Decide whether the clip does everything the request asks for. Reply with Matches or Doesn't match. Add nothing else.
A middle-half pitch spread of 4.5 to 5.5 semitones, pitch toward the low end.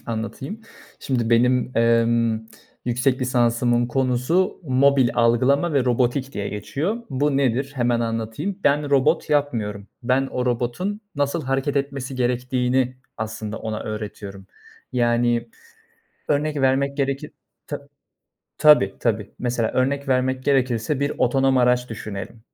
Doesn't match